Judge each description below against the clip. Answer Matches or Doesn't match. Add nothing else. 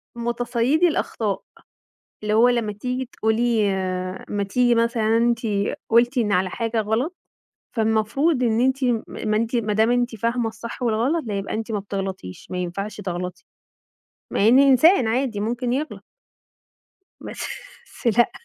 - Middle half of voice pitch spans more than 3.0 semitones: Doesn't match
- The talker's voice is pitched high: Matches